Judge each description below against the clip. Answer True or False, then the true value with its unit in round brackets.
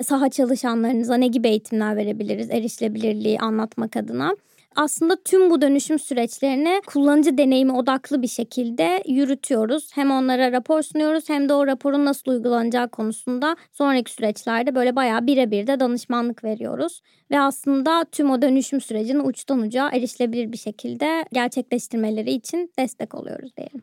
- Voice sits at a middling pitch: False (260 Hz)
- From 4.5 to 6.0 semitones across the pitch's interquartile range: False (3.3 semitones)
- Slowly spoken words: False (140 wpm)